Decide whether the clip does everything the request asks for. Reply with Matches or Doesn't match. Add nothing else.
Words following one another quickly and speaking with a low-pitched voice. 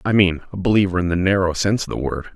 Matches